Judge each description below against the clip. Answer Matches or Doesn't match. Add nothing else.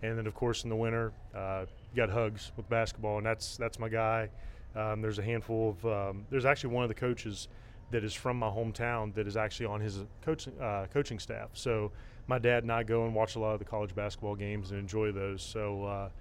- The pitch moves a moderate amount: Doesn't match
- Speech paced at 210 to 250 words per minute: Matches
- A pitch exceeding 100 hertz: Matches